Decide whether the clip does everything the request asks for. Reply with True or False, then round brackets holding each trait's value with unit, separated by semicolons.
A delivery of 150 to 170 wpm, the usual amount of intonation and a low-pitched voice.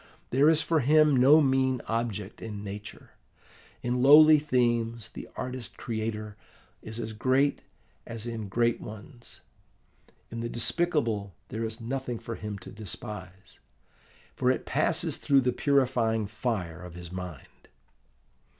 False (135 wpm; 3.6 semitones; 115 Hz)